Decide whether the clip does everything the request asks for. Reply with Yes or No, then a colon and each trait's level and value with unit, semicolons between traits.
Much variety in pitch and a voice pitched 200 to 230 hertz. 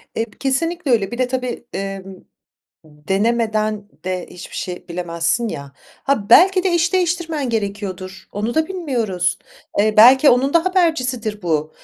Yes: wide, 6.5 semitones; high, 225 Hz